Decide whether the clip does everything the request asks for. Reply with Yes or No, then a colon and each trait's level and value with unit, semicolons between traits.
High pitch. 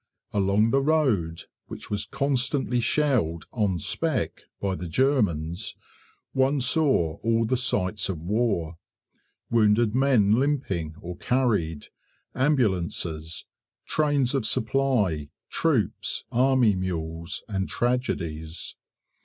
No: low, 110 Hz